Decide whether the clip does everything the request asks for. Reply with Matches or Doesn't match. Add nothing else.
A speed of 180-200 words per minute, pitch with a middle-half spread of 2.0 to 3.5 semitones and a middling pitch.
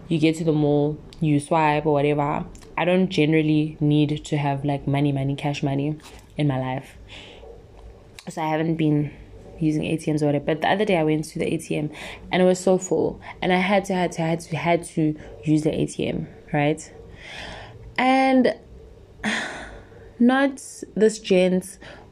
Doesn't match